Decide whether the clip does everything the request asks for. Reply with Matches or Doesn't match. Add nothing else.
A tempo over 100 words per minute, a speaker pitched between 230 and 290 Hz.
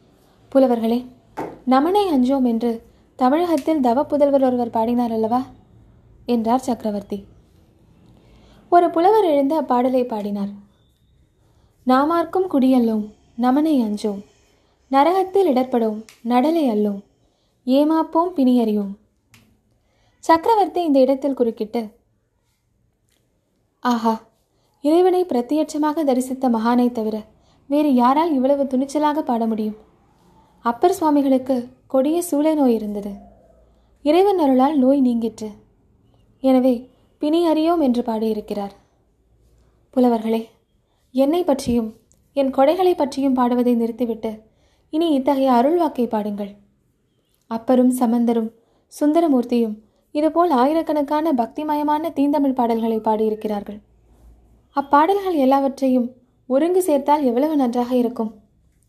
Doesn't match